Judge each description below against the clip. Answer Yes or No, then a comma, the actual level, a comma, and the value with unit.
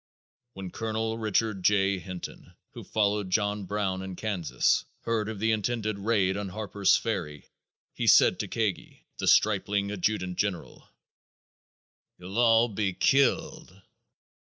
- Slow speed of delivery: Yes, slow, 130 wpm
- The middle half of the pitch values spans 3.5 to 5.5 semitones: No, narrow, 2.4 semitones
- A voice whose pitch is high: No, low, 105 Hz